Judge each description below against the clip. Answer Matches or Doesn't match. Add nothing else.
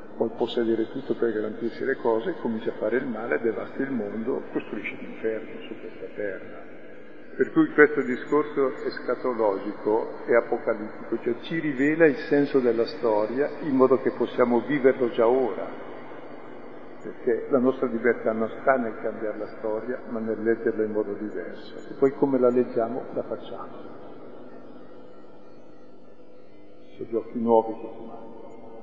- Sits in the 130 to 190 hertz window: Doesn't match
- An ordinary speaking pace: Matches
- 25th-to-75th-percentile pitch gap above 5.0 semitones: Doesn't match